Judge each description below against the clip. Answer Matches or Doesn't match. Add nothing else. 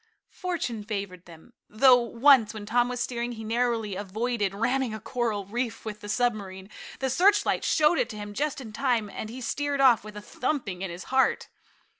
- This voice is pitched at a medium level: Doesn't match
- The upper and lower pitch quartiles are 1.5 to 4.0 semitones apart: Matches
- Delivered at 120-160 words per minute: Doesn't match